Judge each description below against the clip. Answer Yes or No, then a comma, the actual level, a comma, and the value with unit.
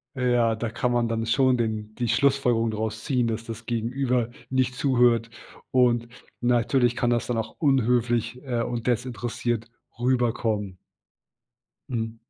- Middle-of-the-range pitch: No, low, 120 Hz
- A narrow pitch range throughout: Yes, narrow, 1.6 semitones